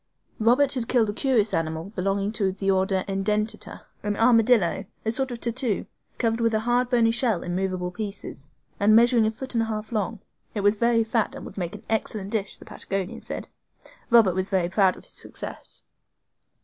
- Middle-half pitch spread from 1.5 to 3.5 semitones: Yes, average, 3.0 semitones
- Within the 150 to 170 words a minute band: No, average, 195 wpm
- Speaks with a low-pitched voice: No, high, 215 Hz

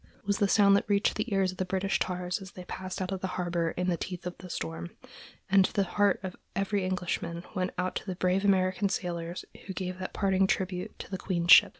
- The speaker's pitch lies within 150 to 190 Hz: Yes, medium, 185 Hz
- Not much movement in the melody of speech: Yes, narrow, 1.4 semitones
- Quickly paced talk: Yes, fast, 235 wpm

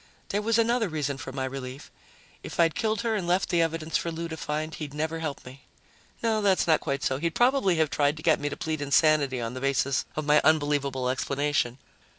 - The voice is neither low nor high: Yes, medium, 155 Hz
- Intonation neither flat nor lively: Yes, average, 3.4 semitones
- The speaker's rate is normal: No, fast, 220 wpm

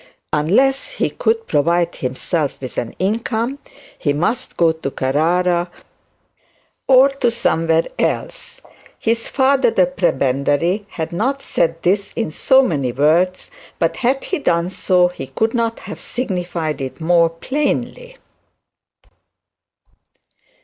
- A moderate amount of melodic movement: No, wide, 7.0 semitones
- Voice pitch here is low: No, medium, 180 Hz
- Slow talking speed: Yes, slow, 115 wpm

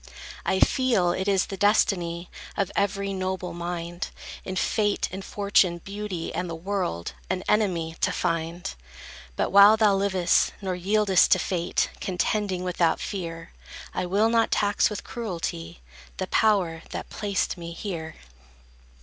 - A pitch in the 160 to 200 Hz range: Yes, medium, 185 Hz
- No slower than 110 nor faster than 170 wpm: Yes, average, 140 wpm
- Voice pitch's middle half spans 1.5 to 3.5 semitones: Yes, average, 2.8 semitones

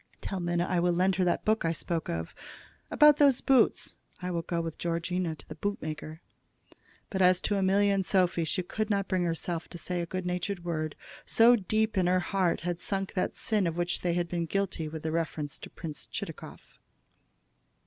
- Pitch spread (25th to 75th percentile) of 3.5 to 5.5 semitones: No, narrow, 2.5 semitones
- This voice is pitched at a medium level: Yes, medium, 180 Hz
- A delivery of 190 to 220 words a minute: Yes, average, 200 wpm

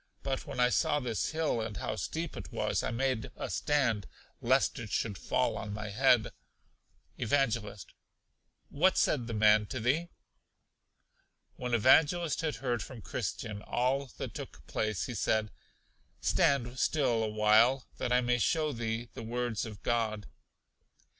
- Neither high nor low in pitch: No, low, 120 Hz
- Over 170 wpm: No, average, 155 wpm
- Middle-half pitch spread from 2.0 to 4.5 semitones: Yes, average, 3.7 semitones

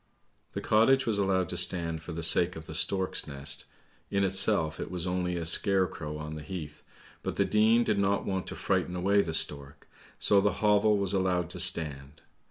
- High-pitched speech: No, very low, 90 Hz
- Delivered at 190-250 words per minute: Yes, average, 200 wpm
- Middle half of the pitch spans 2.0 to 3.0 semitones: No, average, 3.6 semitones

